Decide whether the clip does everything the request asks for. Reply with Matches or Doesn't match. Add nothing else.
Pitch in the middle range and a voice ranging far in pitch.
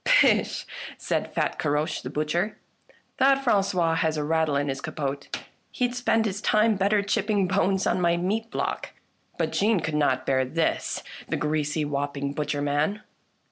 Matches